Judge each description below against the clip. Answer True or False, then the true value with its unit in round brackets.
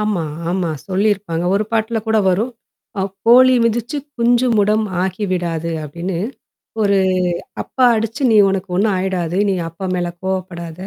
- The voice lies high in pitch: True (195 Hz)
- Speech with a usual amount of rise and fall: True (3.7 semitones)